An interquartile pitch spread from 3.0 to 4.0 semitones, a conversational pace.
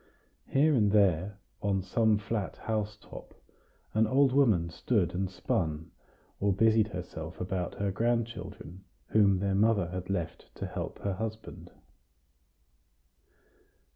No: average, 3.4 semitones; slow, 120 wpm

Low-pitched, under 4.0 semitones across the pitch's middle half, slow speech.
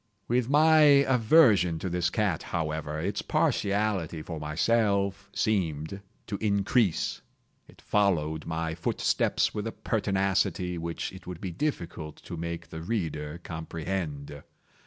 No: very low, 90 Hz; average, 4.4 semitones; slow, 125 wpm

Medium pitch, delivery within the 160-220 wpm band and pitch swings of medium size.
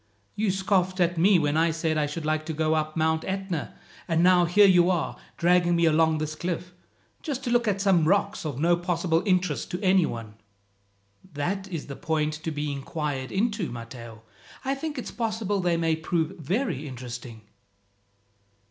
Yes: medium, 165 Hz; average, 180 wpm; average, 3.5 semitones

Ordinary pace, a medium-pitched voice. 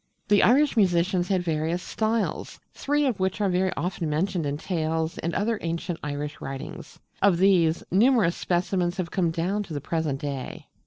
Yes: average, 170 wpm; medium, 175 Hz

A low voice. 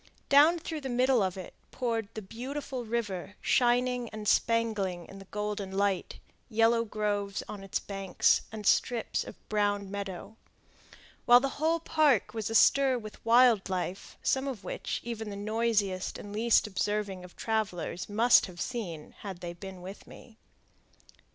No: high, 215 Hz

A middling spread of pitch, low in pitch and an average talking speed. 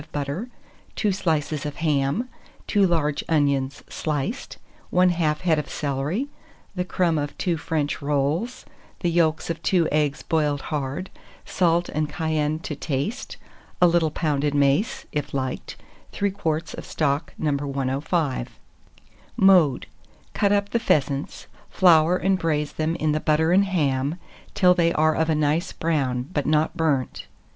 No: average, 3.2 semitones; medium, 155 Hz; average, 150 wpm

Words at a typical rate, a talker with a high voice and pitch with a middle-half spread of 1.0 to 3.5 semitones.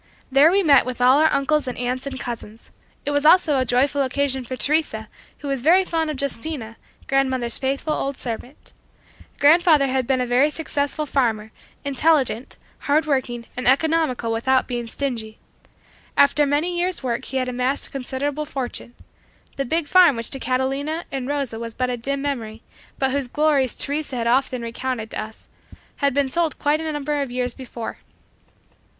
Yes: average, 175 wpm; very high, 270 Hz; average, 2.9 semitones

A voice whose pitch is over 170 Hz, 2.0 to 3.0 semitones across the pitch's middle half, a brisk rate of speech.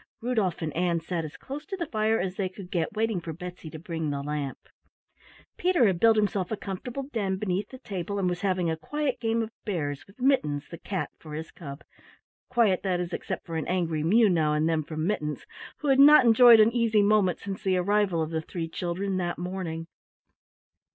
No: medium, 185 Hz; average, 4.8 semitones; fast, 210 wpm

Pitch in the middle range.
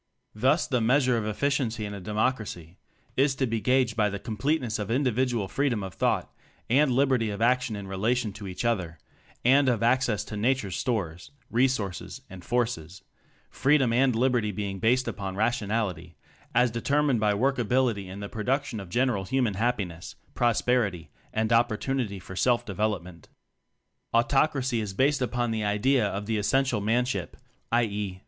No: low, 115 Hz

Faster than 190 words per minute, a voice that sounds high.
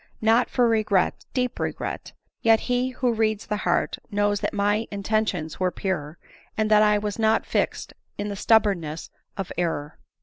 No: average, 165 wpm; high, 210 Hz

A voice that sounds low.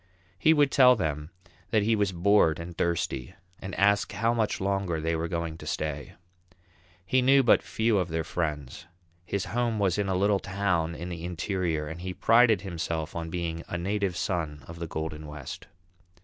Yes: very low, 90 Hz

